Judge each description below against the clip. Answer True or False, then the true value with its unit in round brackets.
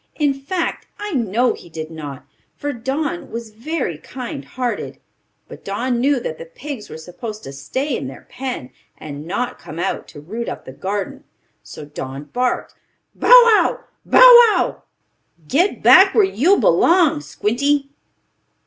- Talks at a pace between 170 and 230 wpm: False (155 wpm)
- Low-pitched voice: False (245 Hz)